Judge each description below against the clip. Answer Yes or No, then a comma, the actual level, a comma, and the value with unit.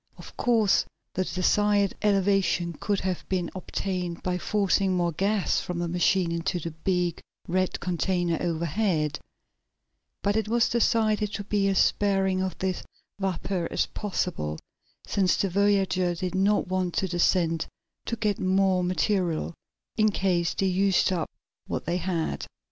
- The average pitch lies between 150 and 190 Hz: Yes, medium, 185 Hz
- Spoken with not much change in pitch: Yes, narrow, 2.3 semitones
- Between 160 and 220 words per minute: No, average, 145 wpm